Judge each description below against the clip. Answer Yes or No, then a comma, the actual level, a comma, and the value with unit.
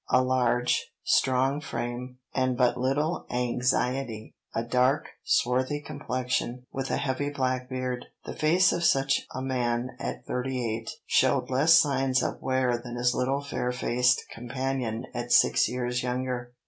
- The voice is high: No, low, 125 Hz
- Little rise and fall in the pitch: Yes, narrow, 1.4 semitones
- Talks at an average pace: Yes, average, 145 wpm